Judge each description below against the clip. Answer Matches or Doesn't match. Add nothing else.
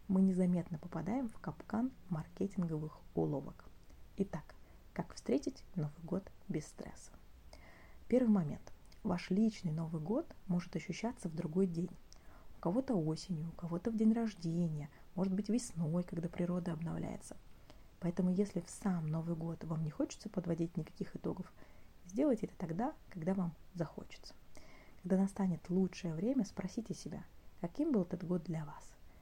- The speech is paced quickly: Doesn't match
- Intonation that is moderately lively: Matches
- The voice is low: Doesn't match